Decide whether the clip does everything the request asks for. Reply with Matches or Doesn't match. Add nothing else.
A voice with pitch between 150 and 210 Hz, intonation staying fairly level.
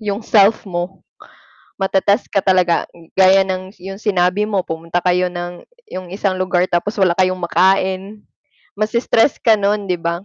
Matches